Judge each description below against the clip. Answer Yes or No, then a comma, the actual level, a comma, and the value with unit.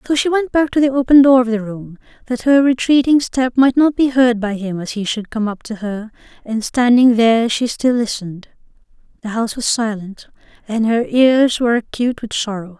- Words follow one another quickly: Yes, fast, 210 wpm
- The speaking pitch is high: Yes, high, 240 Hz